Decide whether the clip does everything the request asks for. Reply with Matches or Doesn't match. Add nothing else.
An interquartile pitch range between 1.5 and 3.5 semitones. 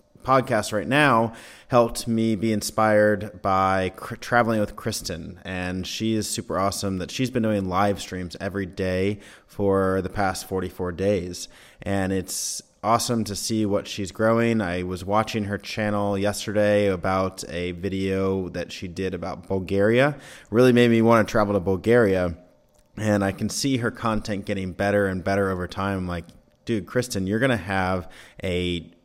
Matches